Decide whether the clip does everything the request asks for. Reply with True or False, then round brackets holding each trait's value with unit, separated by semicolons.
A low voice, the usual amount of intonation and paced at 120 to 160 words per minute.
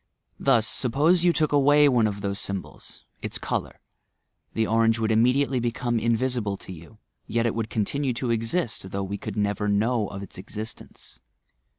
False (115 Hz; 3.6 semitones; 180 wpm)